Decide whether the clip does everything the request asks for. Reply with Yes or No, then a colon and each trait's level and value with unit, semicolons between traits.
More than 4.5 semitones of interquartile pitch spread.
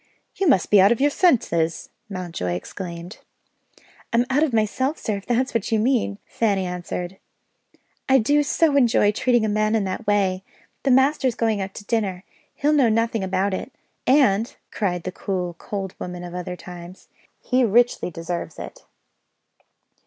Yes: average, 4.9 semitones